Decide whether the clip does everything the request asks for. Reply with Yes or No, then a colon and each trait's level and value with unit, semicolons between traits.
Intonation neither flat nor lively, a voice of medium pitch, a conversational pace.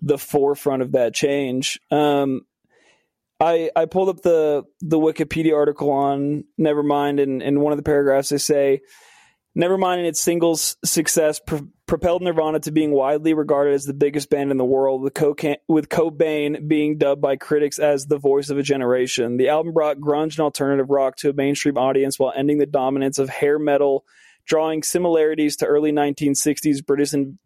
No: narrow, 2.0 semitones; medium, 145 Hz; average, 180 wpm